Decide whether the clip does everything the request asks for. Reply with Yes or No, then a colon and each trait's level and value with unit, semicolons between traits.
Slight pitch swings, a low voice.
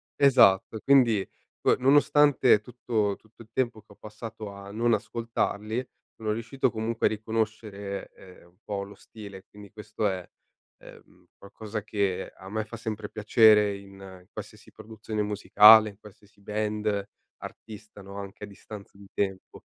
Yes: narrow, 1.8 semitones; low, 105 Hz